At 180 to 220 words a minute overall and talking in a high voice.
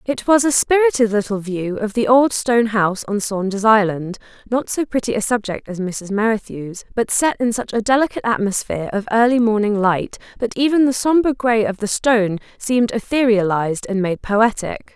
Yes: average, 185 wpm; high, 220 Hz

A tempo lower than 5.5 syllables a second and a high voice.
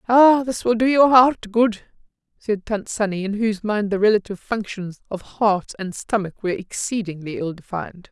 Yes: 5.1 syllables/s; high, 210 Hz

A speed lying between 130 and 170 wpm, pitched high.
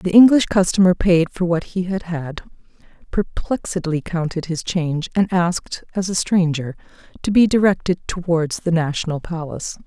No: average, 150 wpm; medium, 175 Hz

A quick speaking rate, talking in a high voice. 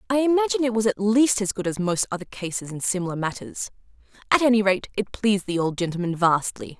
Yes: fast, 210 wpm; high, 205 Hz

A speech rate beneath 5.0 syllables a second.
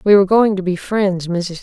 No: 5.2 syllables/s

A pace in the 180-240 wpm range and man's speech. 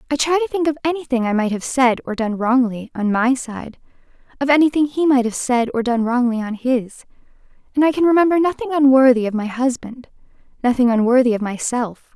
No: average, 195 wpm; female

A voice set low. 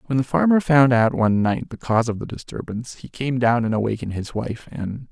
Yes: low, 120 Hz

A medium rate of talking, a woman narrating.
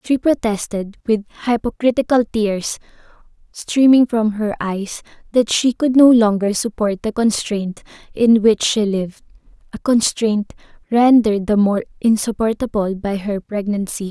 No: slow, 130 wpm; female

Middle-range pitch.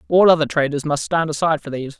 Yes: medium, 155 Hz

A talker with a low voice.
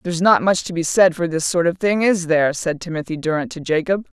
No: medium, 170 Hz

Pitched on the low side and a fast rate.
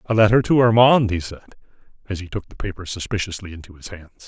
Yes: low, 100 Hz; fast, 210 wpm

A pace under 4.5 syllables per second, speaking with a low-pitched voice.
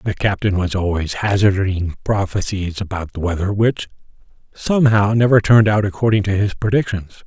No: 5.4 syllables/s; low, 100 Hz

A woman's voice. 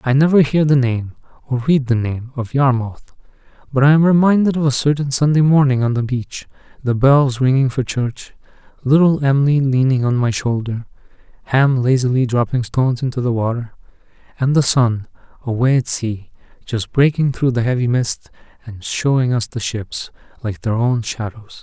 No: male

